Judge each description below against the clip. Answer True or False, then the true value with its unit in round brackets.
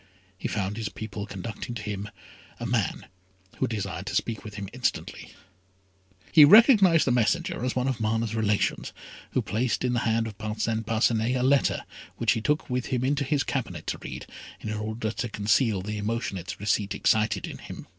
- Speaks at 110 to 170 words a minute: False (185 wpm)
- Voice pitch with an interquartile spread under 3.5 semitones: True (3.1 semitones)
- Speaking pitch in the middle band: False (110 Hz)